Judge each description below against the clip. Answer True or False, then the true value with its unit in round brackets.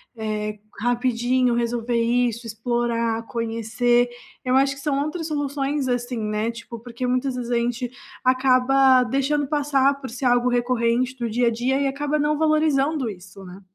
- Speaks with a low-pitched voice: False (245 Hz)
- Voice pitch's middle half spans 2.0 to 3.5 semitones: True (2.6 semitones)